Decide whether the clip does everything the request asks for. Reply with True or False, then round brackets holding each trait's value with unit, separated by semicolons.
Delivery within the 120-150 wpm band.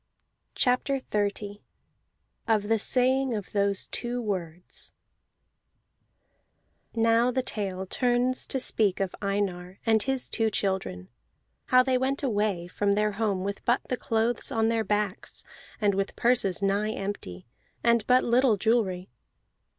True (135 wpm)